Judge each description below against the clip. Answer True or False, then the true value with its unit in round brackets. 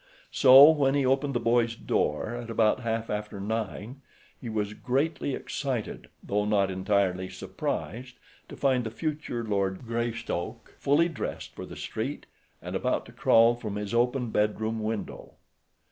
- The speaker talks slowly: False (155 wpm)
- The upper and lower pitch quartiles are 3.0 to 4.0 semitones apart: True (3.6 semitones)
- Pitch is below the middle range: True (115 Hz)